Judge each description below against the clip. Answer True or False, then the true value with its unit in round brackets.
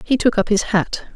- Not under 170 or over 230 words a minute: False (260 wpm)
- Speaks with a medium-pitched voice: False (220 Hz)